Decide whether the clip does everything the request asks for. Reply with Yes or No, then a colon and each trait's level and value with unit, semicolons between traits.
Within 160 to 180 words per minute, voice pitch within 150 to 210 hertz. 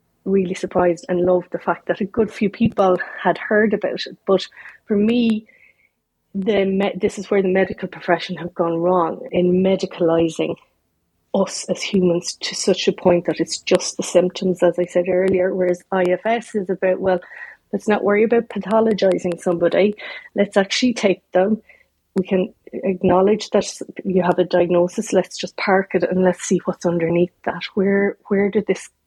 Yes: average, 175 wpm; medium, 185 Hz